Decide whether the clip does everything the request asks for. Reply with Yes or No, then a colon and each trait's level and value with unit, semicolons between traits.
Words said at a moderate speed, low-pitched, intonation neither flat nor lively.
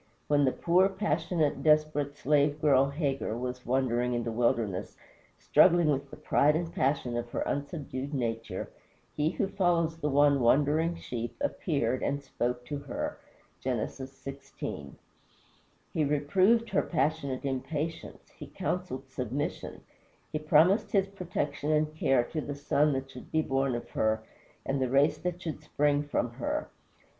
No: average, 150 wpm; medium, 145 Hz; average, 3.3 semitones